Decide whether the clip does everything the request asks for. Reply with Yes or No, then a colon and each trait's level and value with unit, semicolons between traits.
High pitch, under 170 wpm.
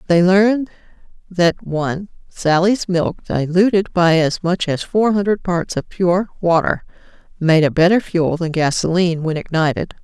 No: medium, 175 Hz; average, 150 wpm